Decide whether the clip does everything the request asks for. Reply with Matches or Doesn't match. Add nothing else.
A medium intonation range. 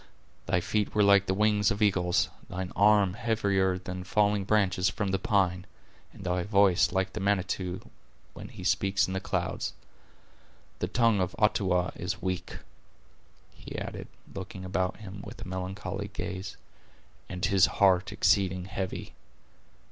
Doesn't match